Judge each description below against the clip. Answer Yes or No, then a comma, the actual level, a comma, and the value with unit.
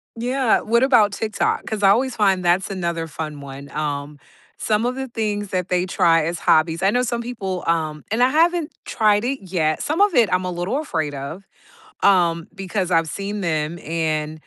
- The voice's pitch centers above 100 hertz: Yes, medium, 185 Hz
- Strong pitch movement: Yes, wide, 5.7 semitones